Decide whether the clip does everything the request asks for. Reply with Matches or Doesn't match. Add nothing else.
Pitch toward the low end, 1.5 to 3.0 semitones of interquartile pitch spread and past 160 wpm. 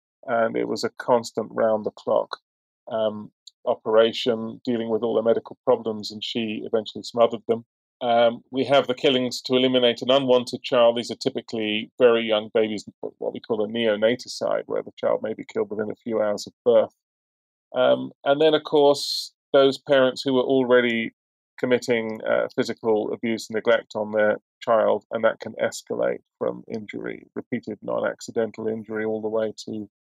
Matches